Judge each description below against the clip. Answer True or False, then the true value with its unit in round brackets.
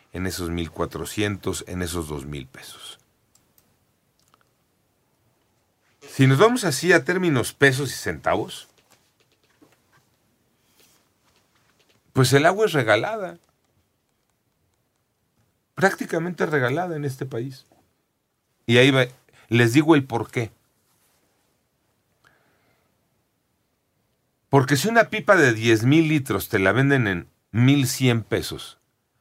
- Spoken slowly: True (90 wpm)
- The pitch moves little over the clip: False (5.3 semitones)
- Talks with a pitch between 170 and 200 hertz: False (125 Hz)